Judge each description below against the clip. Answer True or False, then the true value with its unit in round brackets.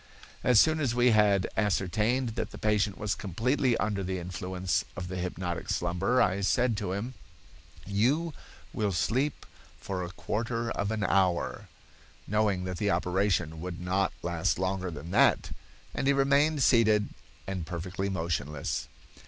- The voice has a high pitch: False (100 Hz)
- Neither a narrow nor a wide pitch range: True (4.1 semitones)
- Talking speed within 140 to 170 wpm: True (150 wpm)